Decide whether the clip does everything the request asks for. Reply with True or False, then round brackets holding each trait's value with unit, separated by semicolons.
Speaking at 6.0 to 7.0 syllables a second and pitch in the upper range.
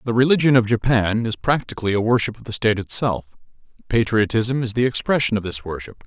False (6.2 syllables/s; 115 Hz)